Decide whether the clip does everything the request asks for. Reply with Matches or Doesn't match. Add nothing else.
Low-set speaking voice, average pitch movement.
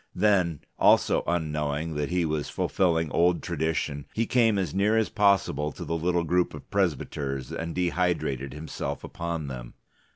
Matches